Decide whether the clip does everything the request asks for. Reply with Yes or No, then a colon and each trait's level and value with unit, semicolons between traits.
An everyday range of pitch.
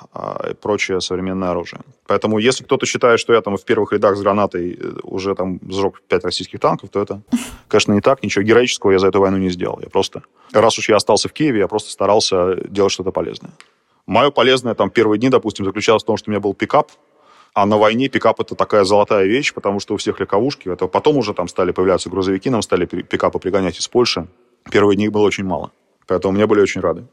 No: narrow, 1.8 semitones